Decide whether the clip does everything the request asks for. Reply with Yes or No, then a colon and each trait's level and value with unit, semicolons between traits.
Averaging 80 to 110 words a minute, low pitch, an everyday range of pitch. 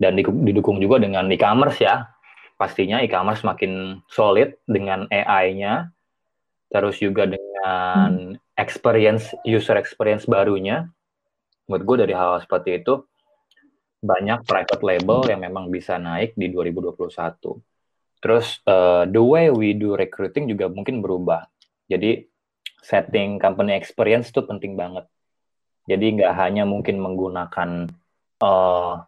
No: average, 120 wpm; low, 100 Hz; average, 4.1 semitones